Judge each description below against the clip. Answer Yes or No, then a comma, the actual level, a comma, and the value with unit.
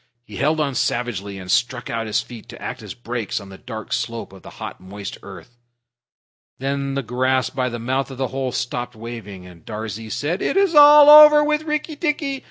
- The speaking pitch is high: No, low, 125 Hz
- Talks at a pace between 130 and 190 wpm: No, fast, 205 wpm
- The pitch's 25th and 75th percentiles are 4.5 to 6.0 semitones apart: Yes, average, 5.1 semitones